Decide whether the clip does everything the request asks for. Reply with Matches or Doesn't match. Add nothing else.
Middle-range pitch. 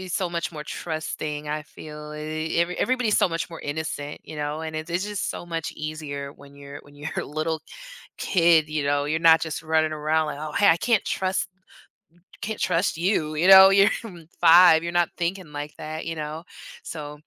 Matches